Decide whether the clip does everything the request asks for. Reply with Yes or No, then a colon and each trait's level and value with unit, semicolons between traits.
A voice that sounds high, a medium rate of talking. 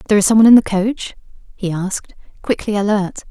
Yes: high, 205 Hz; average, 180 wpm